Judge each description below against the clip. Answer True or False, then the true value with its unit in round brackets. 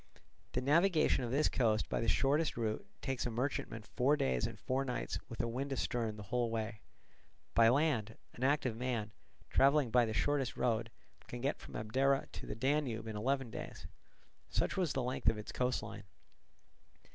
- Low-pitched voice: True (125 Hz)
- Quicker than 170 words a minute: True (180 wpm)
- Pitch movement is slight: False (3.4 semitones)